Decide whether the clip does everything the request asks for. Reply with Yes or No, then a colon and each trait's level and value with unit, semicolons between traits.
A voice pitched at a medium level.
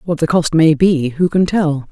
Yes: medium, 160 Hz